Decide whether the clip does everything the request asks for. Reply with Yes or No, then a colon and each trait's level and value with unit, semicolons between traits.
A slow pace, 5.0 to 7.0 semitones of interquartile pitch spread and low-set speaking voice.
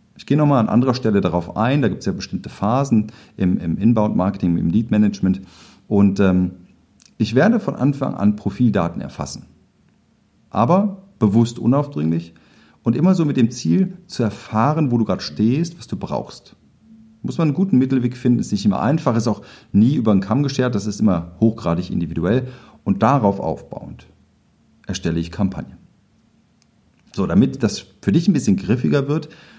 No: average, 170 wpm; wide, 5.5 semitones; low, 110 Hz